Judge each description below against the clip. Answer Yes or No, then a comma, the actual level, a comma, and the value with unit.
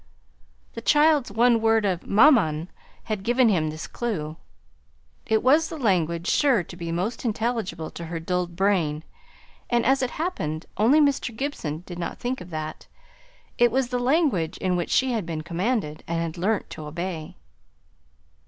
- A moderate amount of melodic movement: No, wide, 6.6 semitones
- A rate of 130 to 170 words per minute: Yes, average, 165 wpm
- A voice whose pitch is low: No, high, 200 Hz